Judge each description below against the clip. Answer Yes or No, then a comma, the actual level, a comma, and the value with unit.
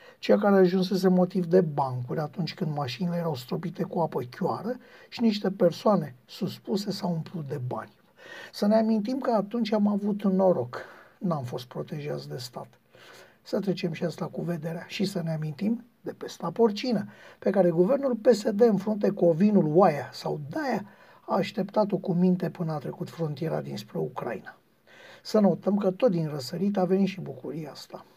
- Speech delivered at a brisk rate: Yes, fast, 175 wpm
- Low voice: No, medium, 185 Hz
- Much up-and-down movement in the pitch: No, average, 3.6 semitones